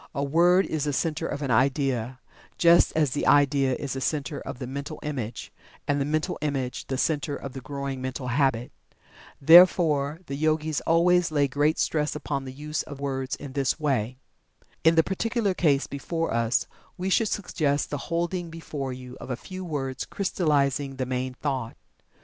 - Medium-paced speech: Yes, average, 180 wpm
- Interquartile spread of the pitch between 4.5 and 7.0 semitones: No, average, 3.1 semitones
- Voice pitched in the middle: Yes, medium, 145 Hz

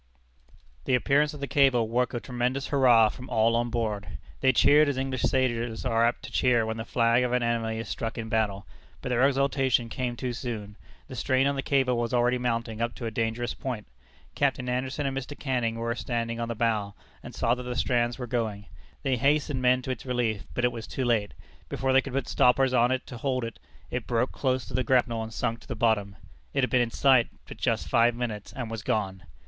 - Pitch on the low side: Yes, low, 120 Hz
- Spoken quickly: Yes, fast, 230 wpm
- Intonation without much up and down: Yes, narrow, 2.1 semitones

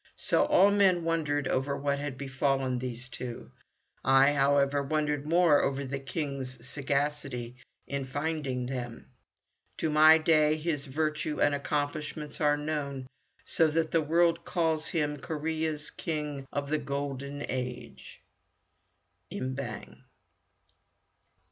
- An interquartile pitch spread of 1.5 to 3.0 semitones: Yes, narrow, 2.4 semitones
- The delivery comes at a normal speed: No, slow, 125 wpm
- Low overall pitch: No, medium, 145 Hz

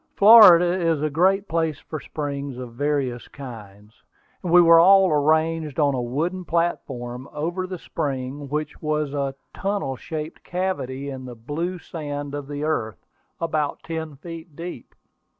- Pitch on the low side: No, medium, 150 Hz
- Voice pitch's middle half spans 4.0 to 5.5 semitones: No, average, 3.6 semitones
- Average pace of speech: Yes, average, 150 wpm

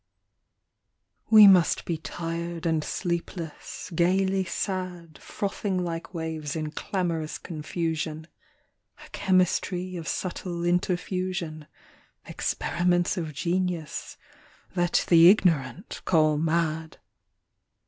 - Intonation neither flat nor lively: No, narrow, 2.2 semitones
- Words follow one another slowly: Yes, slow, 90 wpm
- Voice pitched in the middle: Yes, medium, 170 Hz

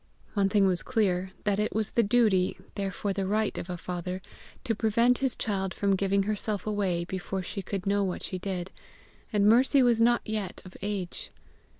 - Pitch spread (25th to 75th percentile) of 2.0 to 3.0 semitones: Yes, narrow, 2.4 semitones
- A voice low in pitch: No, high, 200 Hz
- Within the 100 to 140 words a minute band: No, average, 190 wpm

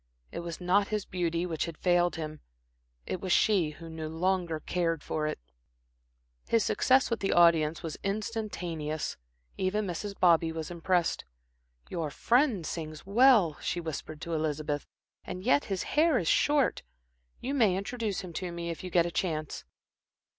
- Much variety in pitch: No, average, 3.7 semitones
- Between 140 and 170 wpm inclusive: Yes, average, 160 wpm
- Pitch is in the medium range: Yes, medium, 175 Hz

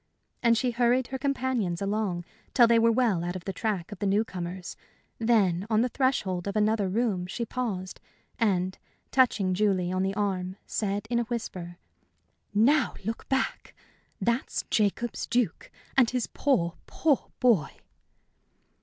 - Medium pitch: No, high, 215 Hz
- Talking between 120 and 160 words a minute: Yes, average, 155 wpm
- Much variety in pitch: No, average, 4.3 semitones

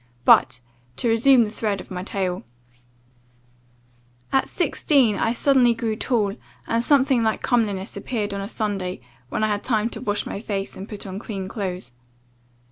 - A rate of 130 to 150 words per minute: No, average, 165 wpm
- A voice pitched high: Yes, high, 215 Hz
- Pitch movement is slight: No, average, 3.1 semitones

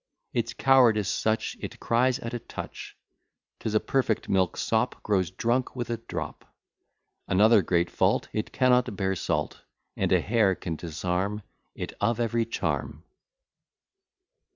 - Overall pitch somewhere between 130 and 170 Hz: No, low, 110 Hz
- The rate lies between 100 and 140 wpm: Yes, slow, 135 wpm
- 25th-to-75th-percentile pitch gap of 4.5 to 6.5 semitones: No, average, 3.8 semitones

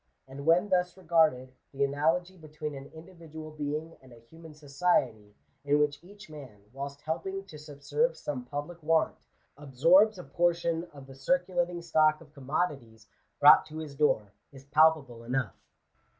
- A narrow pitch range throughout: No, average, 3.5 semitones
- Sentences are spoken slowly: No, average, 150 wpm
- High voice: No, medium, 155 Hz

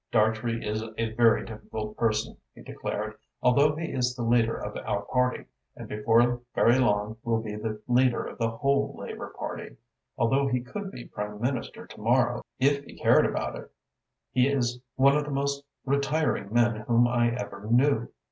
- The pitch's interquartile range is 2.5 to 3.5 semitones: Yes, average, 3.1 semitones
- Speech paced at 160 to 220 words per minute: Yes, average, 175 wpm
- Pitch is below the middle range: Yes, low, 120 Hz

